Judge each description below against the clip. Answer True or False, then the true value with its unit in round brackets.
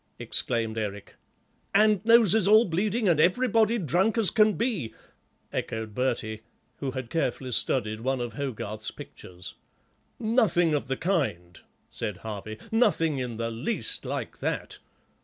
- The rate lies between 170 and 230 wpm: False (135 wpm)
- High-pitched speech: False (140 Hz)